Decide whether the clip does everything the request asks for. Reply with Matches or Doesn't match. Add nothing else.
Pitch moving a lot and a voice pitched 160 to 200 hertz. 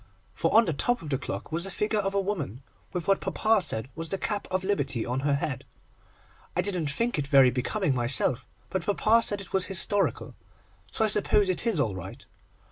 Matches